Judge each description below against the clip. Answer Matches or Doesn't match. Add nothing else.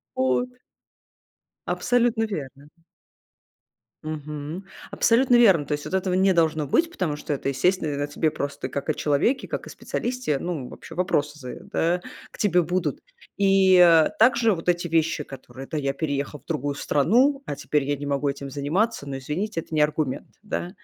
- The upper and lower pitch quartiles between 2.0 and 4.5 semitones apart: Doesn't match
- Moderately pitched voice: Matches